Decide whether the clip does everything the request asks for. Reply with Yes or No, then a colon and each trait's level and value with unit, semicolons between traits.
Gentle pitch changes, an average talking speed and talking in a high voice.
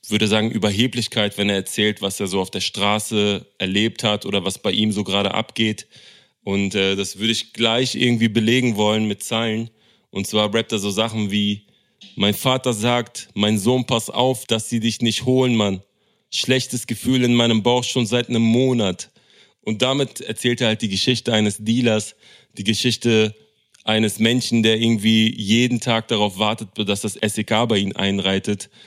No: narrow, 2.3 semitones; average, 180 wpm; low, 110 Hz